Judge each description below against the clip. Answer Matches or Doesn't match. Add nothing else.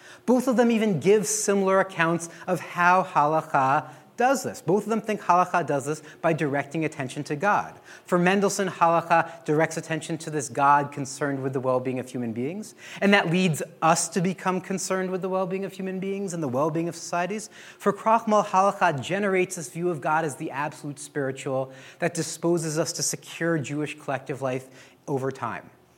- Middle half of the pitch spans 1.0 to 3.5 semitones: Doesn't match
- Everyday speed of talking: Matches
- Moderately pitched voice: Matches